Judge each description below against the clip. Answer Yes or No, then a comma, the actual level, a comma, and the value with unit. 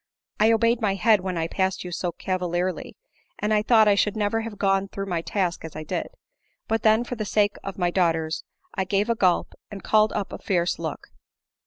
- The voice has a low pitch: No, high, 195 Hz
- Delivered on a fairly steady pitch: No, average, 3.2 semitones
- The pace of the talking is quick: Yes, fast, 215 wpm